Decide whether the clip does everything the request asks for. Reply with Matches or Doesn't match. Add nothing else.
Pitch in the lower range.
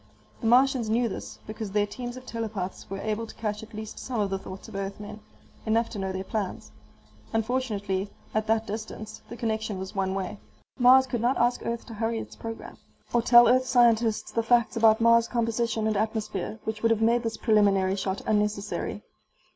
Doesn't match